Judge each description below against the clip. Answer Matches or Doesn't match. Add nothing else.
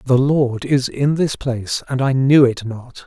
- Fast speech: Matches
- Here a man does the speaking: Matches